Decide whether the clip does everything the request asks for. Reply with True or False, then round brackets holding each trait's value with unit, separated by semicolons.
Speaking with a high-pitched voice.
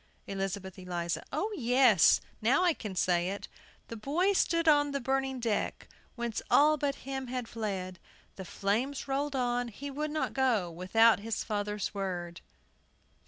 True (235 Hz)